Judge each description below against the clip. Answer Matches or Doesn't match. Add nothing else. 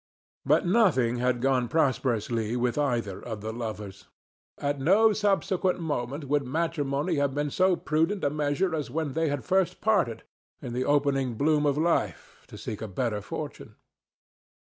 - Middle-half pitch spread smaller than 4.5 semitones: Doesn't match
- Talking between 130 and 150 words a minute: Doesn't match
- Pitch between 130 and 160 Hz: Matches